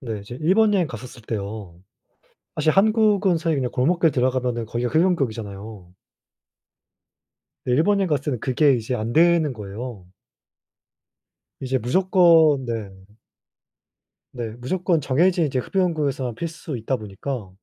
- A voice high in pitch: No, low, 130 Hz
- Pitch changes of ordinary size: No, wide, 6.6 semitones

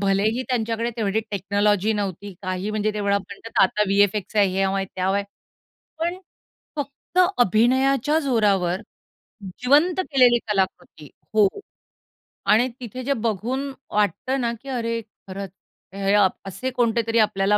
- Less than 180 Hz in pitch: No, high, 210 Hz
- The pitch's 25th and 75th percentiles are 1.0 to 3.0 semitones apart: No, average, 3.8 semitones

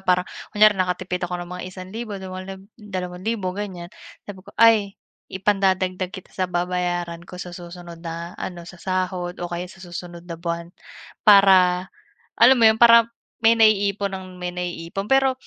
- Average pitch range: No, narrow, 2.1 semitones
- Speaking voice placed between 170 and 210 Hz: Yes, medium, 185 Hz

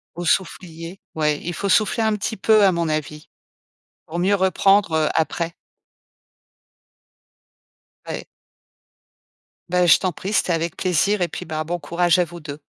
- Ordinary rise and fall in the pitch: Yes, average, 3.3 semitones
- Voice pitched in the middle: Yes, medium, 175 Hz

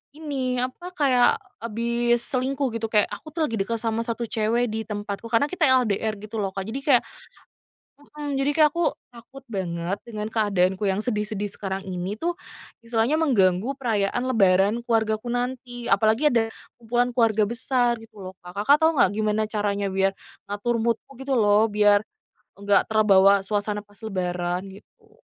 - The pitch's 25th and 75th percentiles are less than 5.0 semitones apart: Yes, average, 3.3 semitones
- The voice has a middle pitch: No, high, 225 Hz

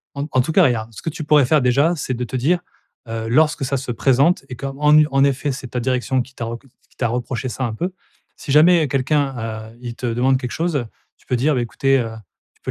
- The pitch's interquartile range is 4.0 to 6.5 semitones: No, average, 3.3 semitones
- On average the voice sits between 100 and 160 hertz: Yes, low, 130 Hz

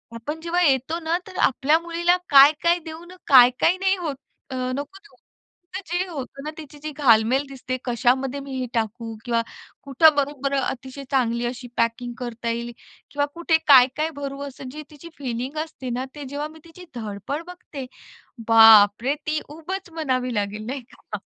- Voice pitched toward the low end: No, very high, 275 Hz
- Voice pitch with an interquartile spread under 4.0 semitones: No, average, 4.3 semitones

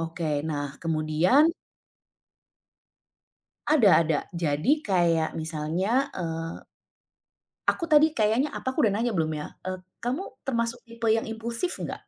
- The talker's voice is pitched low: No, medium, 185 Hz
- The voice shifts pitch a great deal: Yes, wide, 6.9 semitones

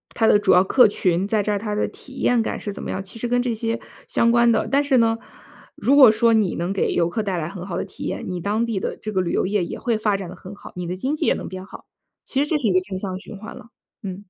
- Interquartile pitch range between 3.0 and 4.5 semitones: Yes, average, 3.6 semitones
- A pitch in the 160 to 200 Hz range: No, high, 210 Hz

